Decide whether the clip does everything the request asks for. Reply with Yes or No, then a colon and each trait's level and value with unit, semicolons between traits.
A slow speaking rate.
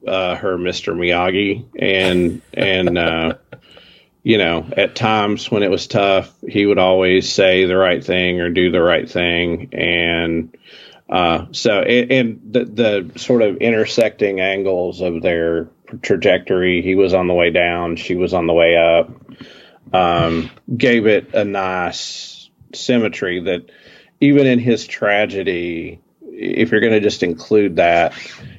No: average, 150 wpm